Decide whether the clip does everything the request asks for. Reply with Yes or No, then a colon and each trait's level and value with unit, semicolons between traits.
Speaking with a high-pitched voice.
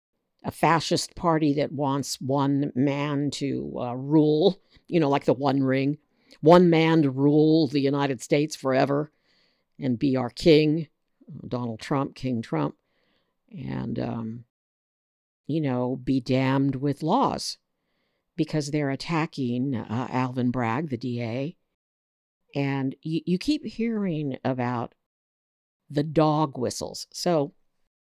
No: medium, 140 Hz